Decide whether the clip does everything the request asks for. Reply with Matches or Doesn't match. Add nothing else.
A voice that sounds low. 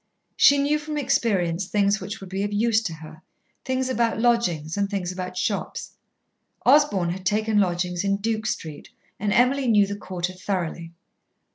Doesn't match